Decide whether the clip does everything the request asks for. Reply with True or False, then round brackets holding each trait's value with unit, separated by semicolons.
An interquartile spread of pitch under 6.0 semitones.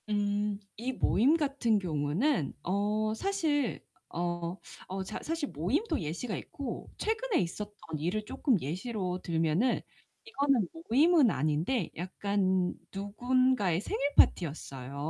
False (6.8 semitones)